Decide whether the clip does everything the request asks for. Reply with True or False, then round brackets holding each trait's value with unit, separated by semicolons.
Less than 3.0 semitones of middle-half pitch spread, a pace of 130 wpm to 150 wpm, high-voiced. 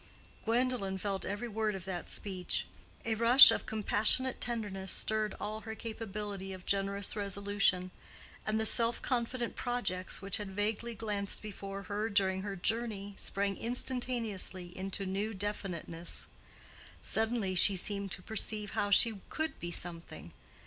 True (2.5 semitones; 140 wpm; 205 Hz)